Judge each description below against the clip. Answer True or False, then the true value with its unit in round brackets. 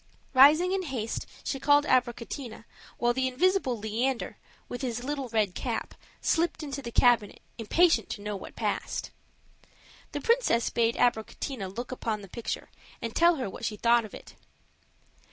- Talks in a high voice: True (245 Hz)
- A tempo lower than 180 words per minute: True (155 wpm)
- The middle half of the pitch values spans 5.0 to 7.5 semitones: False (4.0 semitones)